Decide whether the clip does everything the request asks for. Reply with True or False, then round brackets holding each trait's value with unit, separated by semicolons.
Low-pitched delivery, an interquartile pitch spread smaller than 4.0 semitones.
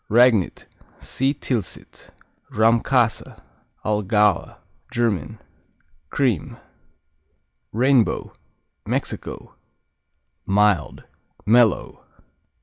True (110 Hz; 2.9 semitones)